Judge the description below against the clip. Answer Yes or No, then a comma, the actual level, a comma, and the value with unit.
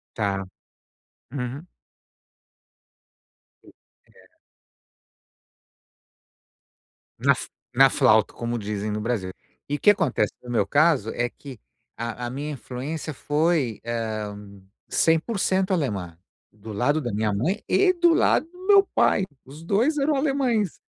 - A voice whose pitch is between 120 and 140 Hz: Yes, low, 135 Hz